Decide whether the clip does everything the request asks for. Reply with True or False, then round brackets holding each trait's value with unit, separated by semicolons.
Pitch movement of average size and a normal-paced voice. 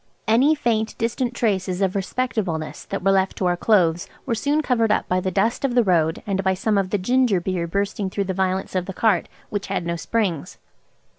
False (3.8 semitones; 215 wpm)